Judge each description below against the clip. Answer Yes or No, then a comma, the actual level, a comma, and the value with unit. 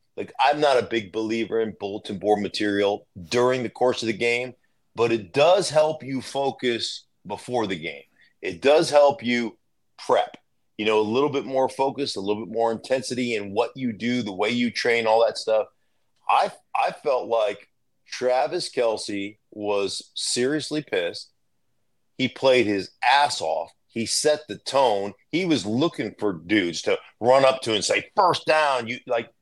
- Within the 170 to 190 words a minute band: Yes, average, 175 wpm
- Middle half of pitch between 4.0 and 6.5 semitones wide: Yes, average, 4.3 semitones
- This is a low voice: Yes, low, 120 Hz